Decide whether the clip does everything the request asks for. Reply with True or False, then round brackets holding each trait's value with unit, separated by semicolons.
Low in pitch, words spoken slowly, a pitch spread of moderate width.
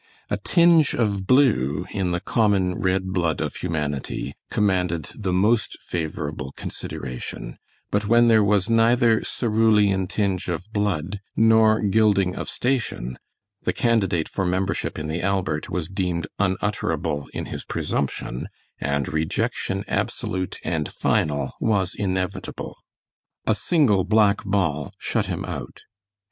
True (95 Hz; 130 wpm; 4.2 semitones)